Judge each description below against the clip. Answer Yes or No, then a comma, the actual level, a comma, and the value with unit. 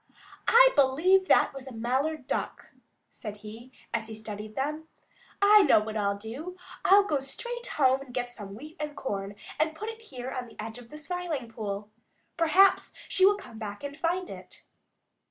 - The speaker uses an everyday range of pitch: No, wide, 7.2 semitones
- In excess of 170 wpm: Yes, average, 190 wpm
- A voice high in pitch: Yes, very high, 270 Hz